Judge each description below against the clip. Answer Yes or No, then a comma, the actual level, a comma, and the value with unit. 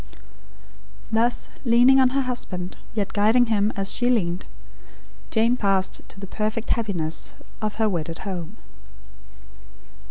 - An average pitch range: Yes, average, 3.8 semitones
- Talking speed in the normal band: No, slow, 125 wpm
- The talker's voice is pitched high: Yes, high, 215 Hz